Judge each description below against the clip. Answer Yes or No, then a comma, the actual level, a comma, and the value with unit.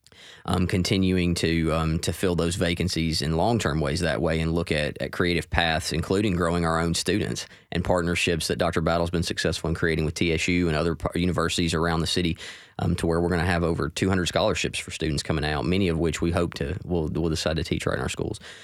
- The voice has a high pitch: No, very low, 85 Hz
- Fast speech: Yes, fast, 230 wpm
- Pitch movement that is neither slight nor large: No, narrow, 1.6 semitones